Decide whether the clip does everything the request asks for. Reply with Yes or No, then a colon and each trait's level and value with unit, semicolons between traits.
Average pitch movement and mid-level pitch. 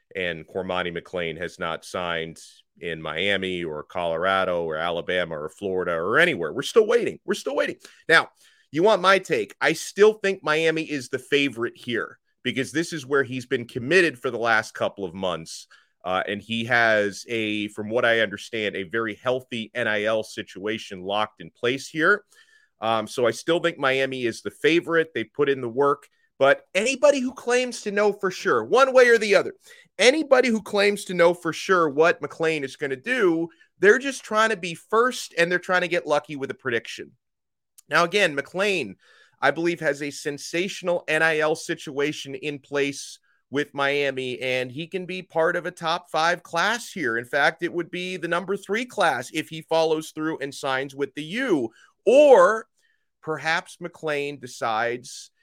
No: wide, 7.7 semitones; medium, 160 Hz